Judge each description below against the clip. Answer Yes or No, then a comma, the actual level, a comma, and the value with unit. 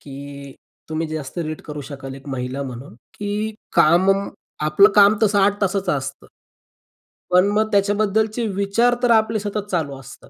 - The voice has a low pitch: No, medium, 185 Hz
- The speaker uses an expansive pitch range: Yes, wide, 6.6 semitones